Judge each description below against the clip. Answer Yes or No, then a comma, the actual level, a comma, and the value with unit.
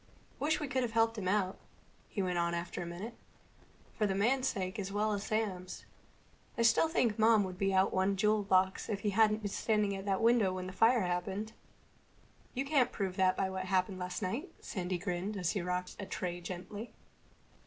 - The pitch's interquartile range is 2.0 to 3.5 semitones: Yes, average, 2.9 semitones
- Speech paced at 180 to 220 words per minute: Yes, fast, 205 wpm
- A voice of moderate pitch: No, high, 195 Hz